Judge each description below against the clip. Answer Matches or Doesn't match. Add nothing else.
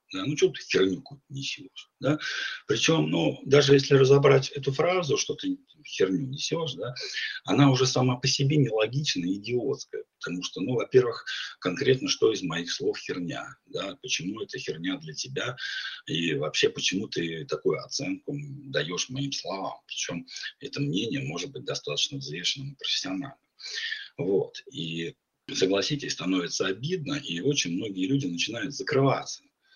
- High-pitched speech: Doesn't match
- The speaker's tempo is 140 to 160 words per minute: Matches